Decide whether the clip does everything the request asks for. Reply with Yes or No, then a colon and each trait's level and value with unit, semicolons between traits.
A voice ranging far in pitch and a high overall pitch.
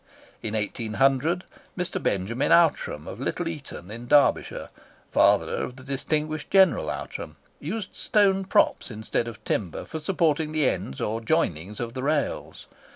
No: wide, 6.5 semitones; medium, 140 Hz